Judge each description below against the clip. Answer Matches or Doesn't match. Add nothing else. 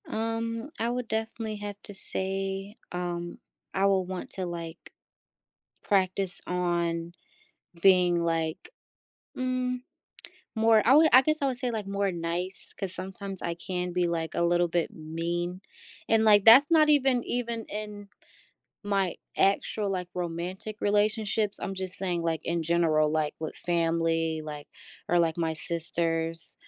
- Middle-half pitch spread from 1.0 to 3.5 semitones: Doesn't match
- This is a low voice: Doesn't match